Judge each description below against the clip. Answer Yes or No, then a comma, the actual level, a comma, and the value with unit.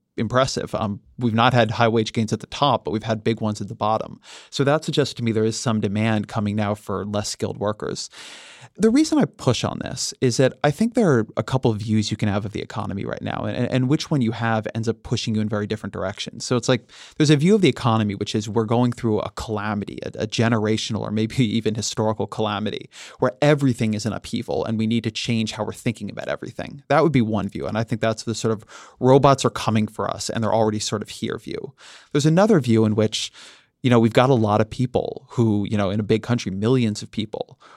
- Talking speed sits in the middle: No, fast, 250 wpm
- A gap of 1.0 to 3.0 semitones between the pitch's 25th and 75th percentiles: Yes, narrow, 2.4 semitones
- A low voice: Yes, low, 110 Hz